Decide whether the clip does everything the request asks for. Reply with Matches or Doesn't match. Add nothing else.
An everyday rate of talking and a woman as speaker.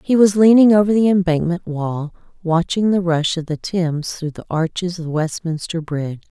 Matches